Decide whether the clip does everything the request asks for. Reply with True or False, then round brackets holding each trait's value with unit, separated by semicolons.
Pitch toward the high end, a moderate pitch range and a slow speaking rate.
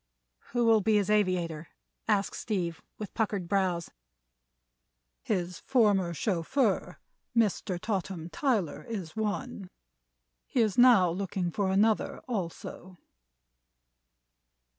True (195 Hz; 3.7 semitones; 100 wpm)